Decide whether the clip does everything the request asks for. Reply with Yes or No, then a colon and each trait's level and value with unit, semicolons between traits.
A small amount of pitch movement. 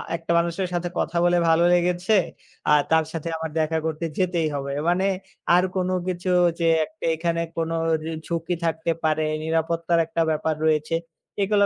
Yes: narrow, 1.6 semitones